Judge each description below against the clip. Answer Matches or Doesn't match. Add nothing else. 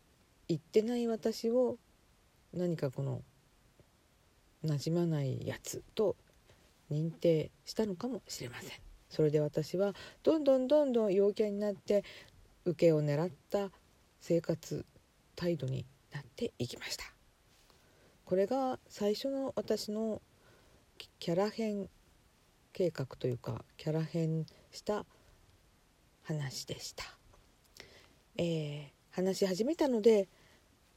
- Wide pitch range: Matches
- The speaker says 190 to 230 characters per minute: Matches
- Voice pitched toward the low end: Doesn't match